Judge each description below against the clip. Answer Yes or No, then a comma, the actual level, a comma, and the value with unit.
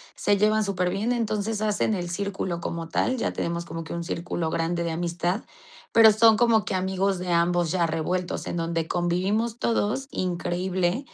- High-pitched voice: No, medium, 180 Hz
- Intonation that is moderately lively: Yes, average, 3.7 semitones